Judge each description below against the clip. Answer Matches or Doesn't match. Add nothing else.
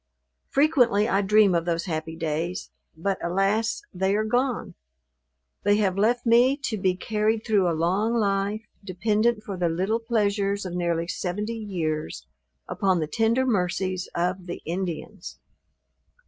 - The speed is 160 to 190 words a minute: Doesn't match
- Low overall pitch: Doesn't match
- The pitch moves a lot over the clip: Doesn't match